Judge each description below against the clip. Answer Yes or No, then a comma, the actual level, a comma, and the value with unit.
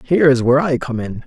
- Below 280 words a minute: No, fast, 285 wpm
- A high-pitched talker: No, low, 135 Hz